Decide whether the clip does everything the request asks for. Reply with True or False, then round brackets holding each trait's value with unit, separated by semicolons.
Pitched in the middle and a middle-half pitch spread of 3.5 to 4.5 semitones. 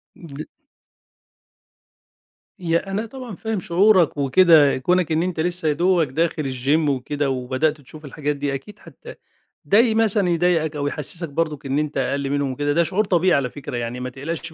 True (155 Hz; 4.1 semitones)